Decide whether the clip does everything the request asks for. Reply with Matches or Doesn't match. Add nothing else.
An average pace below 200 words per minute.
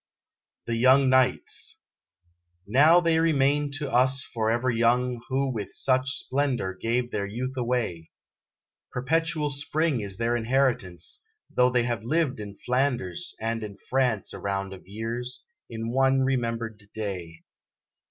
Matches